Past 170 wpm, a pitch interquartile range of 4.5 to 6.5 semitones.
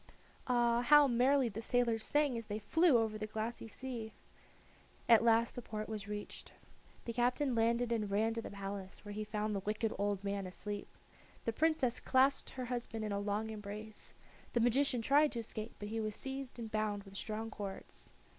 No: average, 190 wpm; narrow, 2.6 semitones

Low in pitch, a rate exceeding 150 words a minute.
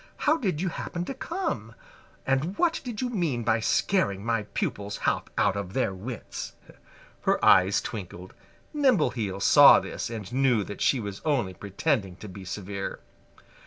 Yes: low, 115 Hz; average, 160 wpm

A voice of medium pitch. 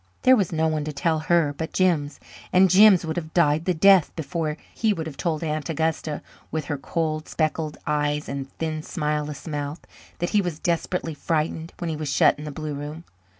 Yes: medium, 155 Hz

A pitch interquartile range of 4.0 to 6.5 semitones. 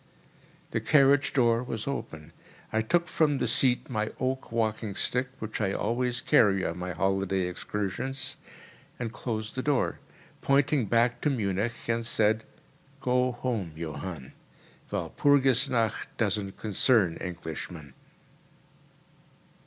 Yes: average, 4.8 semitones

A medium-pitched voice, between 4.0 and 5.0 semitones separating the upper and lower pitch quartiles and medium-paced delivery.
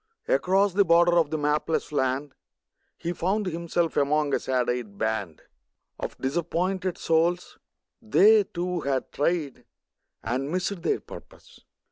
No: medium, 165 Hz; average, 4.5 semitones; slow, 130 wpm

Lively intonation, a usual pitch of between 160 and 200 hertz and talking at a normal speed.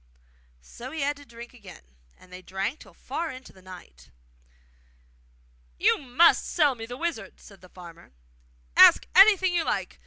No: wide, 8.7 semitones; high, 245 Hz; average, 165 wpm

